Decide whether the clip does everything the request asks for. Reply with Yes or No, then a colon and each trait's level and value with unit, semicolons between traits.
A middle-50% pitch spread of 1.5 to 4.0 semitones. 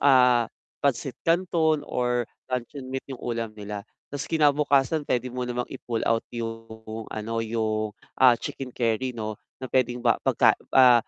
Yes: average, 2.7 semitones